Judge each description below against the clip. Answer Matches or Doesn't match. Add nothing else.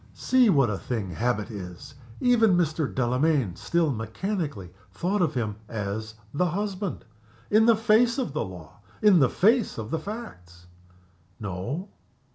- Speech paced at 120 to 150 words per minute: Matches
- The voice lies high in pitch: Doesn't match